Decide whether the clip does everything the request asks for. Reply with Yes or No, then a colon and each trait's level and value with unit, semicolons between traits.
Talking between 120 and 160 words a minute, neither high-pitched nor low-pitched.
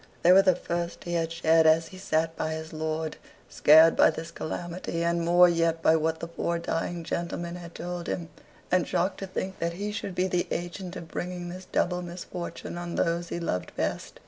No: fast, 205 wpm; medium, 170 Hz